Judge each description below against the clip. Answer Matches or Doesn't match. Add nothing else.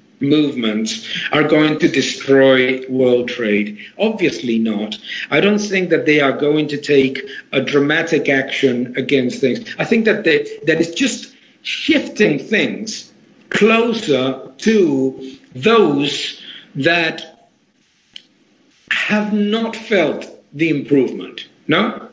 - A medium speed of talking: Doesn't match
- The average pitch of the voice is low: Doesn't match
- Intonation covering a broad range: Matches